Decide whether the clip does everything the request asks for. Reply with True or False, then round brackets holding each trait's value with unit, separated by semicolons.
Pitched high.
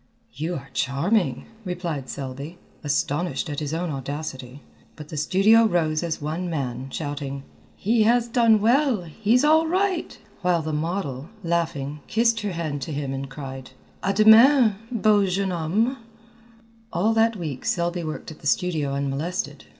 False (170 Hz)